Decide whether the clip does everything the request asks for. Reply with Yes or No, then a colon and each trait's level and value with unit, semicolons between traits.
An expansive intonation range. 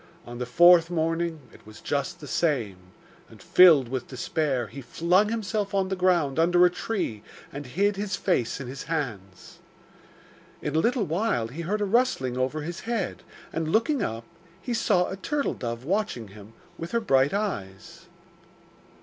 Yes: wide, 7.3 semitones